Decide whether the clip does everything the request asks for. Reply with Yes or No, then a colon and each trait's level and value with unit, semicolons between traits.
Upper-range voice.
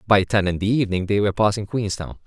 No: low, 100 Hz